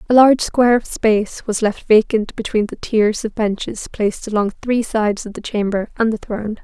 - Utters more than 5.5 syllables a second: No, 5.2 syllables/s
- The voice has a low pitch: No, high, 220 Hz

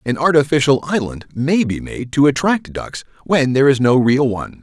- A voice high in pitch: No, low, 135 Hz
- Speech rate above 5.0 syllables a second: Yes, 5.2 syllables/s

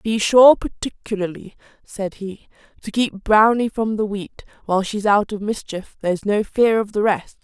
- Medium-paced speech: Yes, average, 180 wpm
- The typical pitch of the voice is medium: No, high, 210 Hz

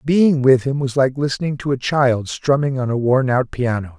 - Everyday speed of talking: No, fast, 225 wpm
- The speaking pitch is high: No, low, 130 Hz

